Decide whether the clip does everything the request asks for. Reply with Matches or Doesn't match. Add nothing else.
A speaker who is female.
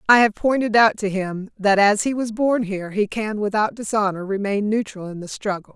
Matches